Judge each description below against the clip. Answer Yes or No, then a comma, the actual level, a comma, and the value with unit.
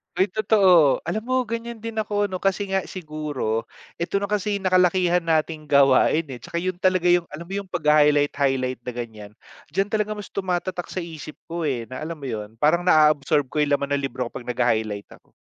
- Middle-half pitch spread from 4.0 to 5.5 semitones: Yes, average, 5.1 semitones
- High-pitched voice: No, medium, 165 Hz